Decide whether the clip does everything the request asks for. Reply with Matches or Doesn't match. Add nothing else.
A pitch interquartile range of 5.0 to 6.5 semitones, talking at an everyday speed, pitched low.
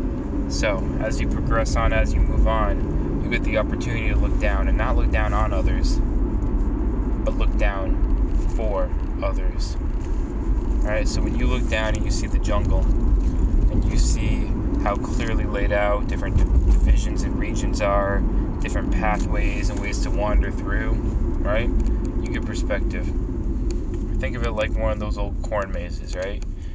Matches